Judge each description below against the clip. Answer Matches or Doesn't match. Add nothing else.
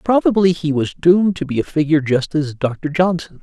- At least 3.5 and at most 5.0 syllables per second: Doesn't match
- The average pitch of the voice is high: Doesn't match